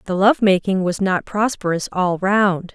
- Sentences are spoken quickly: No, average, 175 wpm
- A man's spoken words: No, female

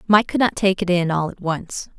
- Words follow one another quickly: Yes, fast, 270 wpm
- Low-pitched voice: No, medium, 185 Hz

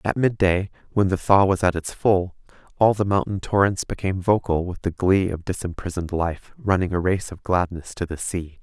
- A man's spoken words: Yes, male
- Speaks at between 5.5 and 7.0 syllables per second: No, 5.3 syllables/s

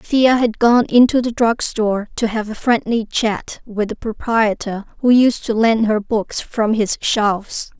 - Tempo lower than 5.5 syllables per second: Yes, 4.1 syllables/s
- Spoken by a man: No, female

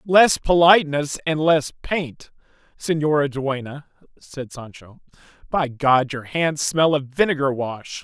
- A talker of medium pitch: Yes, medium, 145 Hz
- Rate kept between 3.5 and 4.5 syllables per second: Yes, 3.9 syllables/s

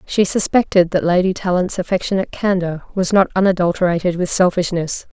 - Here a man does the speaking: No, female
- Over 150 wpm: No, average, 140 wpm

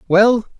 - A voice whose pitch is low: No, high, 215 Hz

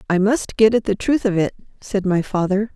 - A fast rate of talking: Yes, fast, 240 wpm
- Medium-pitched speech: No, high, 205 Hz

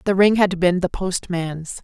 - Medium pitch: Yes, medium, 180 Hz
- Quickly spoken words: No, average, 195 wpm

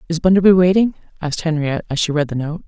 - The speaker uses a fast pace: Yes, fast, 225 wpm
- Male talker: No, female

